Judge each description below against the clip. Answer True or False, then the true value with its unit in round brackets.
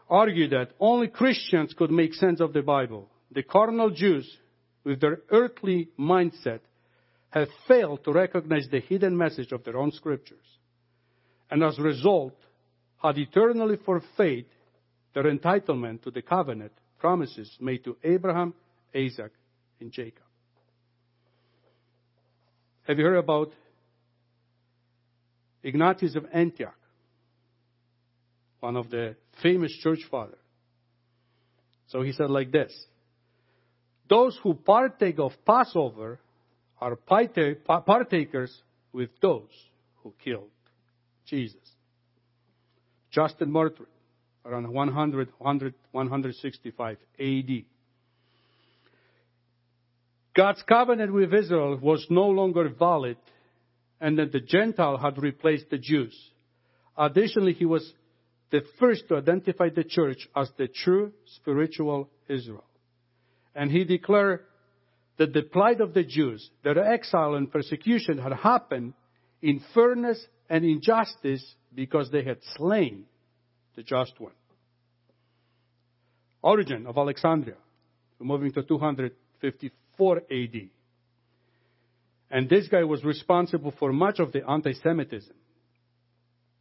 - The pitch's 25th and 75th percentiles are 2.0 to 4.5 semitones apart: False (5.1 semitones)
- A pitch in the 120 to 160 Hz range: True (135 Hz)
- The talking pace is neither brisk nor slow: False (110 wpm)